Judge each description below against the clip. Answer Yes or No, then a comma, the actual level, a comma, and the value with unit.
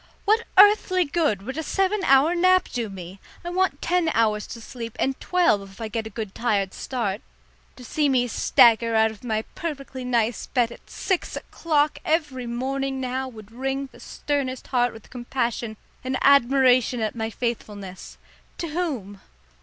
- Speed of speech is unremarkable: Yes, average, 170 wpm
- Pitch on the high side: Yes, very high, 250 Hz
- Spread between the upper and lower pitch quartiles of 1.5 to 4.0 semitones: No, average, 4.7 semitones